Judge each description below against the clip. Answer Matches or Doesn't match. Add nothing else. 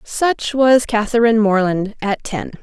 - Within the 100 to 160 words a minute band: Matches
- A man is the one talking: Doesn't match